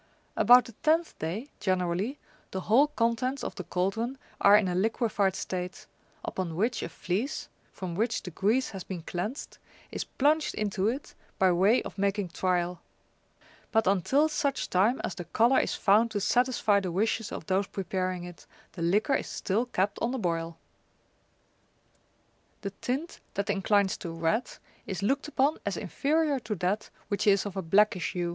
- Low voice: No, high, 205 Hz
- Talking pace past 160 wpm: Yes, average, 170 wpm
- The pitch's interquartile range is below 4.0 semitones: No, average, 4.7 semitones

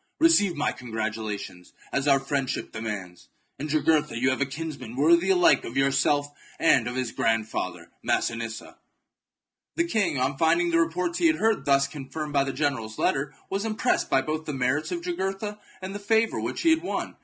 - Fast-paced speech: No, average, 185 wpm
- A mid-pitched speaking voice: Yes, medium, 145 Hz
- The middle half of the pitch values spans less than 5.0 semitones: No, average, 5.3 semitones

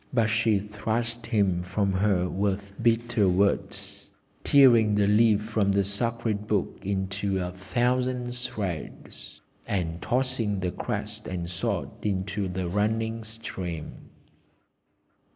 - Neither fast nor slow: No, slow, 115 wpm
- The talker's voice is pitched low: Yes, low, 105 Hz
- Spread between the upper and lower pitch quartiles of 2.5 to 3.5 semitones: Yes, average, 3.0 semitones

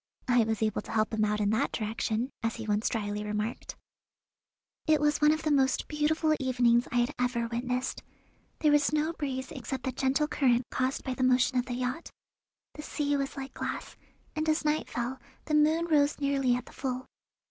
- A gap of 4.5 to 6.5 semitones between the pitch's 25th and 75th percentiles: No, average, 3.9 semitones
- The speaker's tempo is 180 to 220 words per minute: Yes, average, 200 wpm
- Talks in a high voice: Yes, very high, 260 Hz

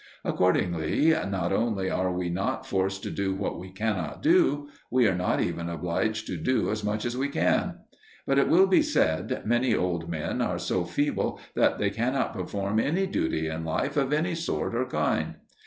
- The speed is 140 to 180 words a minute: No, average, 190 wpm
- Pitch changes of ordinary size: No, wide, 6.4 semitones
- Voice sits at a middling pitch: No, low, 100 Hz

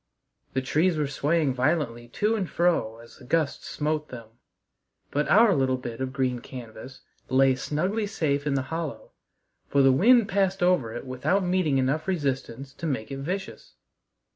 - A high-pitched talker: No, medium, 140 Hz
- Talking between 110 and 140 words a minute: No, average, 165 wpm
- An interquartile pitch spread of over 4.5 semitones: Yes, average, 5.2 semitones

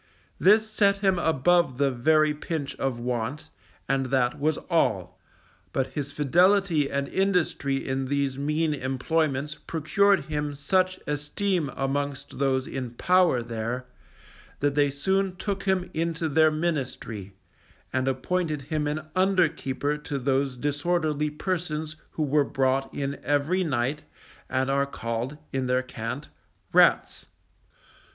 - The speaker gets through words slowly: Yes, slow, 130 wpm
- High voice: No, medium, 145 Hz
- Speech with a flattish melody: No, average, 3.7 semitones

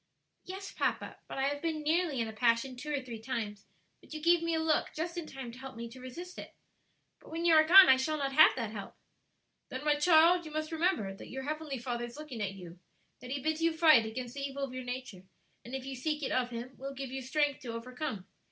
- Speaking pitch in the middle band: No, very high, 270 Hz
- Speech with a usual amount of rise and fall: Yes, average, 4.1 semitones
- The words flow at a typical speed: No, fast, 255 wpm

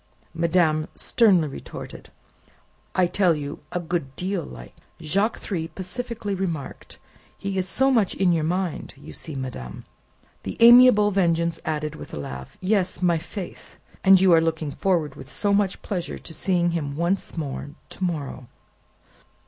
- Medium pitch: Yes, medium, 175 Hz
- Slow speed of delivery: No, average, 155 wpm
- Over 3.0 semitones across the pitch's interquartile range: Yes, average, 3.7 semitones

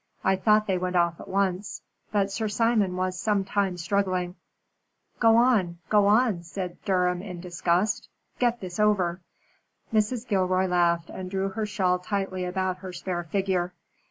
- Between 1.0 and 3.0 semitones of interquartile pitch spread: Yes, narrow, 2.4 semitones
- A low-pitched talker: No, high, 190 Hz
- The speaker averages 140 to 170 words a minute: Yes, average, 155 wpm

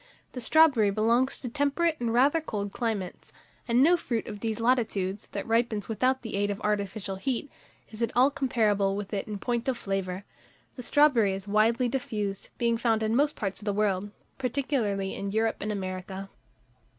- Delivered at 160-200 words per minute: Yes, average, 180 wpm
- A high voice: Yes, high, 220 Hz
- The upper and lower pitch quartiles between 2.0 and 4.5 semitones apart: Yes, average, 3.8 semitones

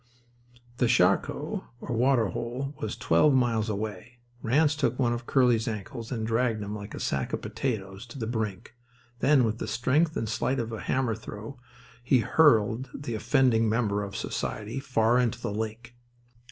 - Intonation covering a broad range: No, average, 2.7 semitones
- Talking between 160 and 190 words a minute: Yes, average, 170 wpm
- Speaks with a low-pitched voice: Yes, low, 115 Hz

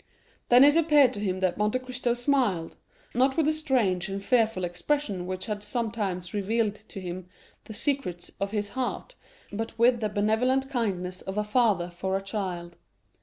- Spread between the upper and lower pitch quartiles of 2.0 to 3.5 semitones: No, average, 4.9 semitones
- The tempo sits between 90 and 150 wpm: No, average, 170 wpm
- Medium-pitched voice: No, high, 210 Hz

